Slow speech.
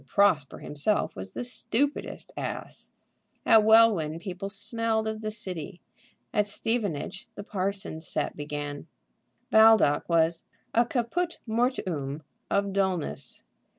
Yes: slow, 115 wpm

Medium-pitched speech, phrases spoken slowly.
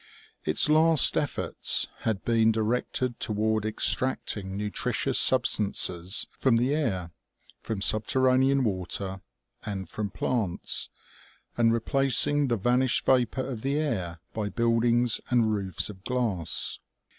No: low, 115 Hz; slow, 120 wpm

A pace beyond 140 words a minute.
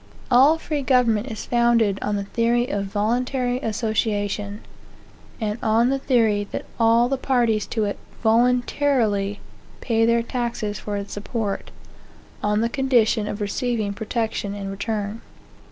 No: slow, 135 wpm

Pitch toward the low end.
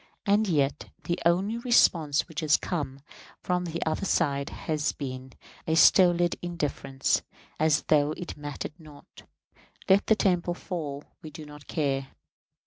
No: medium, 155 Hz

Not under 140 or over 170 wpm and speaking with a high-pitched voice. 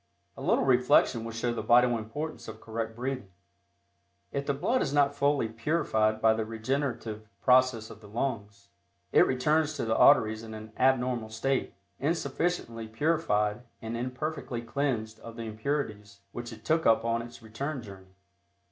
No: average, 160 wpm; low, 115 Hz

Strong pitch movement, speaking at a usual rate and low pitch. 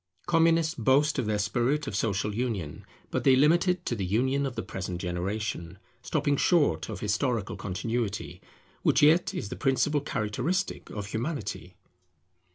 Yes: wide, 6.2 semitones; average, 155 wpm; low, 120 Hz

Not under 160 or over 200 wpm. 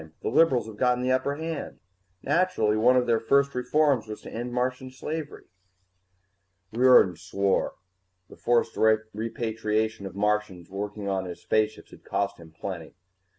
No: average, 150 wpm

